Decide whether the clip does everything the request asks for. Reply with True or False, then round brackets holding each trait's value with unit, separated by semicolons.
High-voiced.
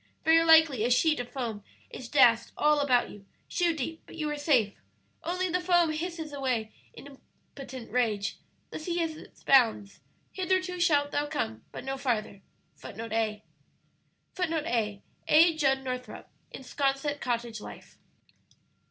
True (275 Hz)